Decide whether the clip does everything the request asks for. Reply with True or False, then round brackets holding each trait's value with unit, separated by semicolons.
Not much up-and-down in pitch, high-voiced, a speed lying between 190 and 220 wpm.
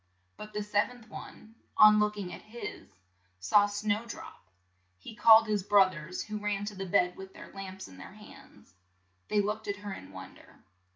True (1.8 semitones; 205 Hz; 195 wpm)